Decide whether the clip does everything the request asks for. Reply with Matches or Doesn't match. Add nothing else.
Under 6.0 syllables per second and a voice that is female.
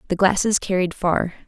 Matches